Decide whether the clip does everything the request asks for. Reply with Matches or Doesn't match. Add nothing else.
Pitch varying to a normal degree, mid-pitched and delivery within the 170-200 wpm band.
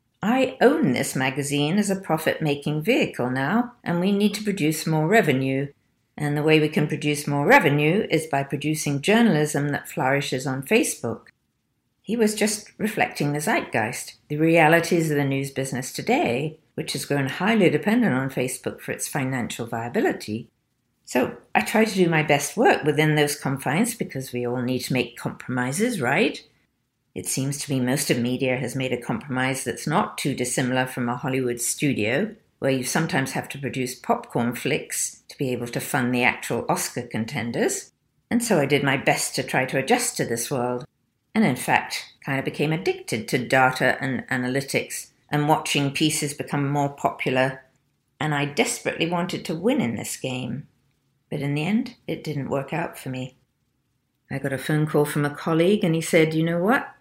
Matches